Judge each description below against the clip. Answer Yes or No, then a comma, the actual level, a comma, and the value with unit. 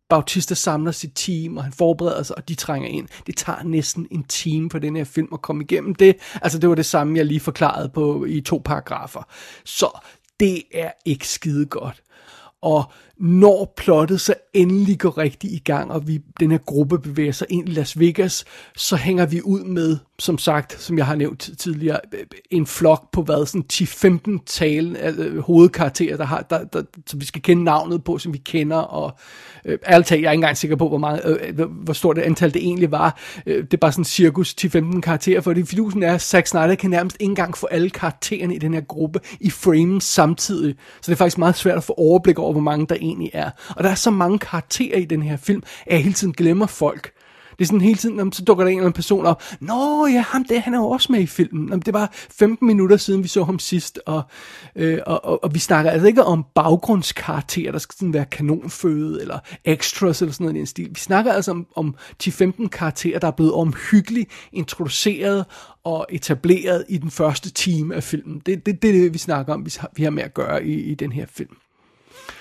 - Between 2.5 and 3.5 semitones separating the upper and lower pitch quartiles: Yes, average, 3.0 semitones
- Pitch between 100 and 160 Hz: No, medium, 170 Hz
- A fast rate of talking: Yes, fast, 230 wpm